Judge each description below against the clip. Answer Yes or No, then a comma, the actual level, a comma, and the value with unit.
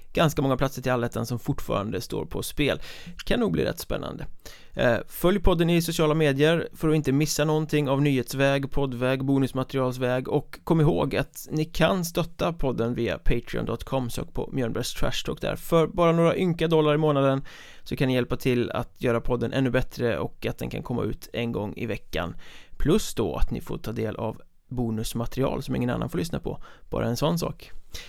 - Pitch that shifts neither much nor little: Yes, average, 3.9 semitones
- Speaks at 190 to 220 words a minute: Yes, fast, 195 wpm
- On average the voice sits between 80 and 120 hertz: No, low, 135 Hz